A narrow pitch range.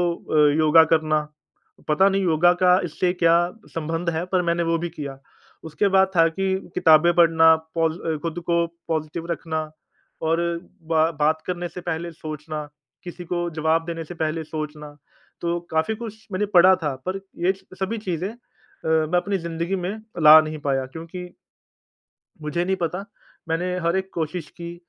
Yes: narrow, 2.1 semitones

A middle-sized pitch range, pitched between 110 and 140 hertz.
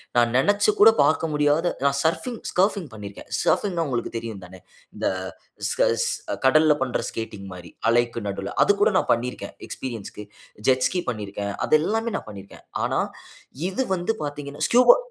No: wide, 8.4 semitones; low, 135 Hz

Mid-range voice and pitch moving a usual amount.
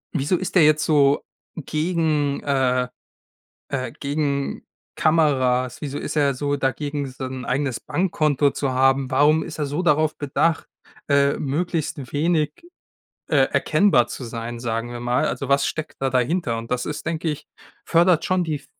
Yes: medium, 145 Hz; average, 3.1 semitones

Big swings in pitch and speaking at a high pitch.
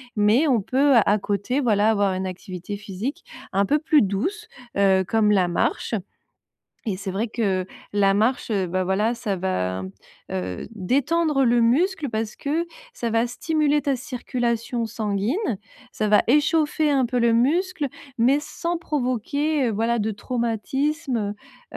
Yes: wide, 5.8 semitones; high, 230 Hz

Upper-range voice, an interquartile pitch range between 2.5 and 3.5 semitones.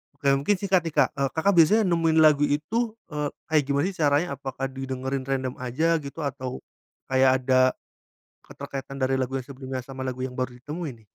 No: medium, 140 Hz; average, 3.2 semitones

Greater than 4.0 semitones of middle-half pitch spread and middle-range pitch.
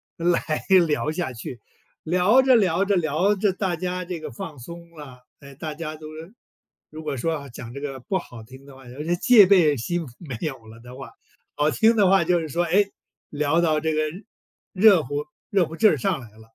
Yes: average, 4.5 semitones; medium, 160 Hz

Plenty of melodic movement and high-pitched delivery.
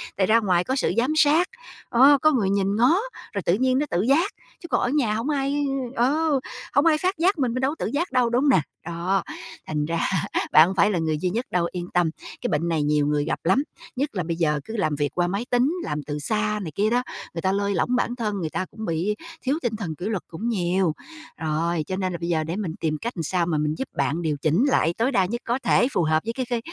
Yes: wide, 7.0 semitones; high, 200 Hz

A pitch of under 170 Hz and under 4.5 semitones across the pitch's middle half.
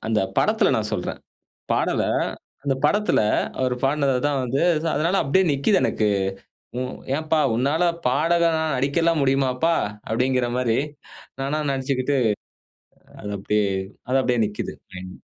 Yes: low, 135 Hz; average, 3.7 semitones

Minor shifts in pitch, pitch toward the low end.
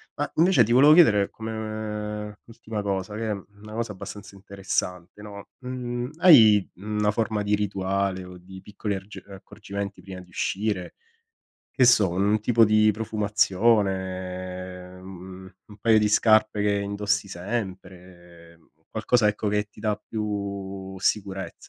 Yes: narrow, 2.2 semitones; low, 105 Hz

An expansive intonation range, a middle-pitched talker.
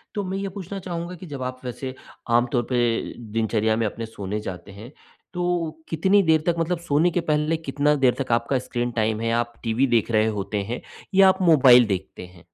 No: wide, 6.7 semitones; low, 130 Hz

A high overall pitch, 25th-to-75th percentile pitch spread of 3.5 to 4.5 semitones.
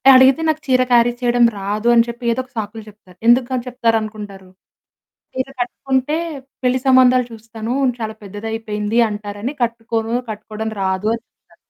No: high, 230 Hz; average, 2.8 semitones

